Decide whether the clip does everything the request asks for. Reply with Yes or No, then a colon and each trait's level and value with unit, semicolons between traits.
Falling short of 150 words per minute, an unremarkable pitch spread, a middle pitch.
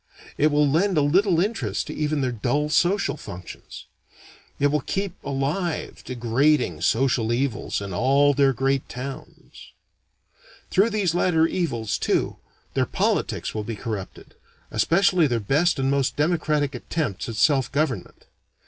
Yes: average, 140 wpm; average, 4.7 semitones; medium, 145 Hz